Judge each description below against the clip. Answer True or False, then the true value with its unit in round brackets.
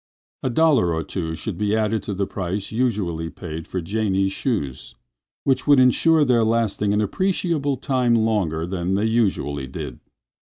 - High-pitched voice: False (105 Hz)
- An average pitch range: False (6.0 semitones)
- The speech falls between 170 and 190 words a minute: False (160 wpm)